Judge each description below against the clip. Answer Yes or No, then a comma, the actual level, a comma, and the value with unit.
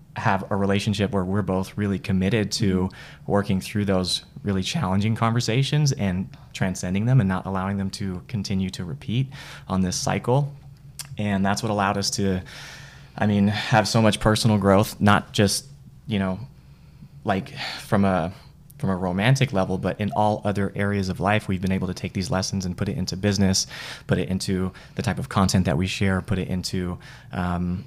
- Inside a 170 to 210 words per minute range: Yes, average, 185 wpm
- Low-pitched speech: Yes, low, 100 Hz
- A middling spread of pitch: Yes, average, 3.2 semitones